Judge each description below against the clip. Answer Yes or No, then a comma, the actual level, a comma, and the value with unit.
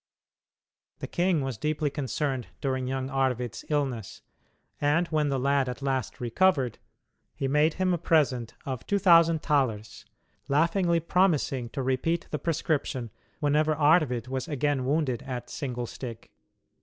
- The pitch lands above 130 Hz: Yes, medium, 140 Hz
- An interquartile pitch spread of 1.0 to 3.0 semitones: No, average, 3.5 semitones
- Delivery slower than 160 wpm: Yes, average, 140 wpm